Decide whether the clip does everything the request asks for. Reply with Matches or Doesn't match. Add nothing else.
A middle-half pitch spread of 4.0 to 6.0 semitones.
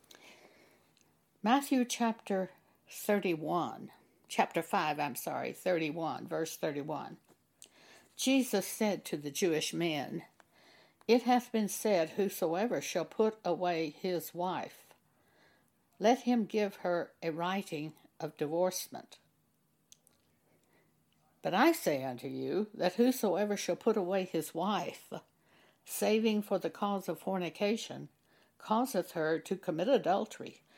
Matches